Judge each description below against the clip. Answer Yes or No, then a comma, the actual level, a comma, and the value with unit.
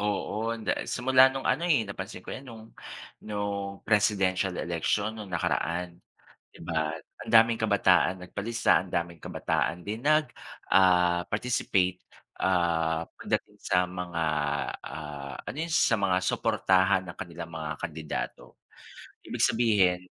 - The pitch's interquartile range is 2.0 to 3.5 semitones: No, average, 4.2 semitones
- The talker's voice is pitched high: No, very low, 95 Hz